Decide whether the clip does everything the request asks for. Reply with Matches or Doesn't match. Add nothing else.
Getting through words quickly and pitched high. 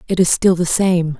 Doesn't match